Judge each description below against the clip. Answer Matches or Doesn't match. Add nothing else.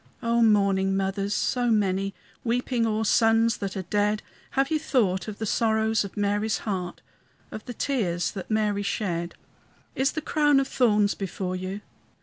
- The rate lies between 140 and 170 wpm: Matches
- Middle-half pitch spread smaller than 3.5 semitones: Matches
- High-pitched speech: Matches